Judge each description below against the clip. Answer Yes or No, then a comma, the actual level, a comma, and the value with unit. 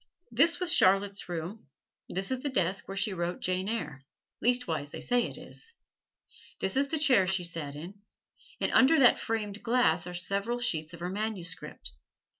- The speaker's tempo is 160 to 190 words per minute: Yes, average, 175 wpm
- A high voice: Yes, high, 195 Hz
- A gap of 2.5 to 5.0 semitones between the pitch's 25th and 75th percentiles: No, wide, 5.5 semitones